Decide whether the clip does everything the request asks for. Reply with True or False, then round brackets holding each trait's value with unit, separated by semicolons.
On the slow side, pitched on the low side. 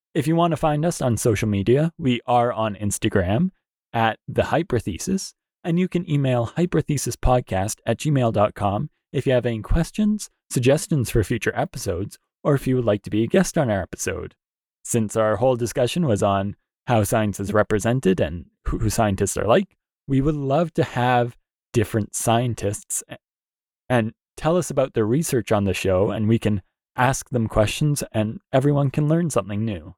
False (170 wpm; 120 Hz)